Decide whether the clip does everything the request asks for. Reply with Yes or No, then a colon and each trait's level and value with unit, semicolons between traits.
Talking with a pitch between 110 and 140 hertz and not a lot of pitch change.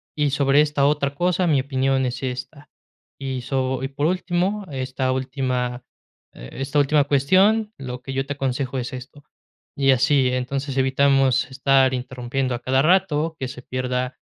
Yes: low, 135 Hz; narrow, 1.9 semitones